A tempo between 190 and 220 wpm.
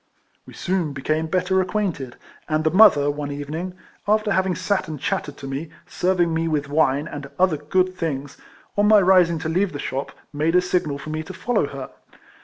Yes: average, 195 wpm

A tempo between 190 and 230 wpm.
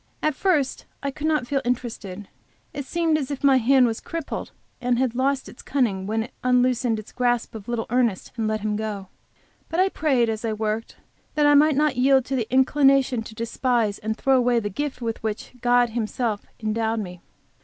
Yes: average, 200 wpm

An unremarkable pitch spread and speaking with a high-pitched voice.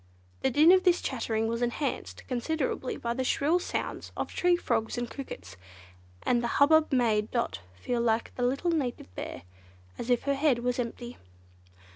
Yes: average, 3.6 semitones; high, 245 Hz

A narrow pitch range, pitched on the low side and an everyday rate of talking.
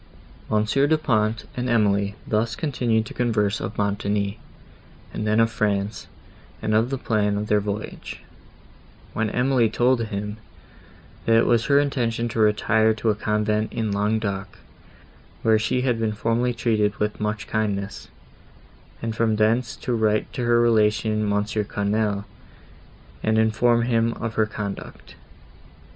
Yes: narrow, 1.7 semitones; low, 110 Hz; average, 145 wpm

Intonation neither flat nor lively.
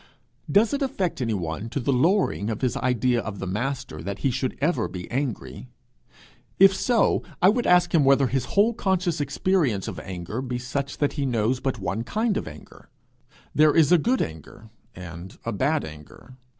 No: wide, 8.1 semitones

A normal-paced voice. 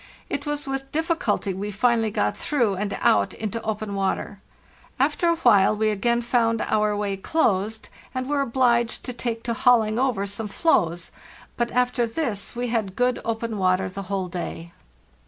Yes: average, 170 wpm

